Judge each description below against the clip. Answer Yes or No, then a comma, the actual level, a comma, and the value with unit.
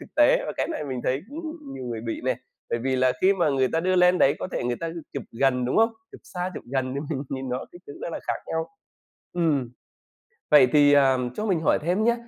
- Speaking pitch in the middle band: Yes, medium, 145 Hz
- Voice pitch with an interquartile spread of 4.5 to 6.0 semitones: Yes, wide, 5.5 semitones